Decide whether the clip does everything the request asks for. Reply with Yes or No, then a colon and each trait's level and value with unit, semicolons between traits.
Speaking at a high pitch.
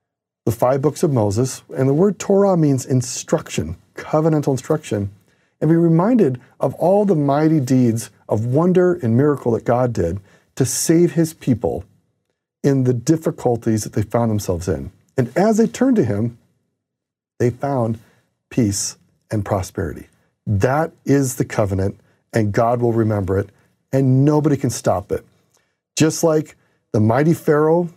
No: low, 130 Hz